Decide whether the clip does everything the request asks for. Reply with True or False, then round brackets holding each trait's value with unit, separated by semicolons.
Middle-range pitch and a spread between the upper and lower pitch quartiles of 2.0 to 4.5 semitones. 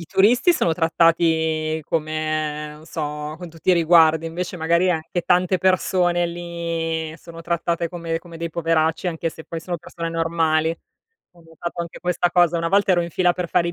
False (165 Hz; 1.4 semitones)